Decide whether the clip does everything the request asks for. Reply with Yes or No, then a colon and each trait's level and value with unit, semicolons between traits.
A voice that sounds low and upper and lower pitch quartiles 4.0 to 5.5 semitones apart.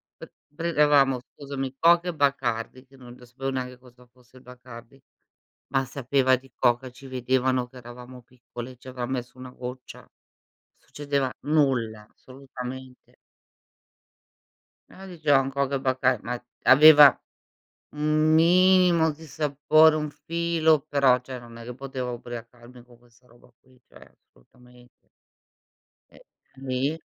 No: low, 130 Hz; narrow, 2.6 semitones